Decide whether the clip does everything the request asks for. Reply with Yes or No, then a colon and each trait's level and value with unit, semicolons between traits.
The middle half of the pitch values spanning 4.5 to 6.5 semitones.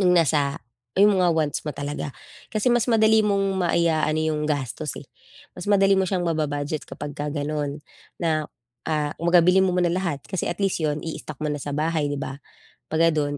No: average, 3.9 semitones